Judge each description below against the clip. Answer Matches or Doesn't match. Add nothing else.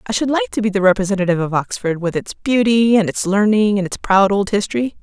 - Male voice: Doesn't match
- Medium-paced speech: Doesn't match